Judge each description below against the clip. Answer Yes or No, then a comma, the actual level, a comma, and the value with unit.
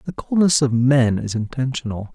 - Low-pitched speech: Yes, low, 130 Hz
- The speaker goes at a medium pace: Yes, average, 170 wpm